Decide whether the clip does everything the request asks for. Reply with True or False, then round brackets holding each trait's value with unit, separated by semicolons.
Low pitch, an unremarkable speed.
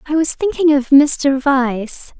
False (285 Hz; 165 wpm)